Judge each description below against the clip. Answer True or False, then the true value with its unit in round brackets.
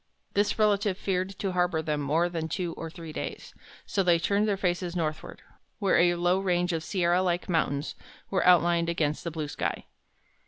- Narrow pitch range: True (2.3 semitones)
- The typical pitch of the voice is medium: True (175 Hz)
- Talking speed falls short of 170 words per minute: False (185 wpm)